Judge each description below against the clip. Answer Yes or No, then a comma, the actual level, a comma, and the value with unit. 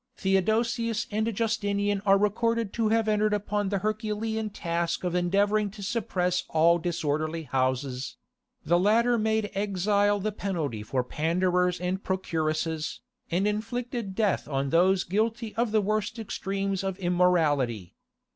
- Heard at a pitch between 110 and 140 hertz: No, high, 195 Hz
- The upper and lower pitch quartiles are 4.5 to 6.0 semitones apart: No, average, 3.8 semitones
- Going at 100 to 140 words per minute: Yes, slow, 135 wpm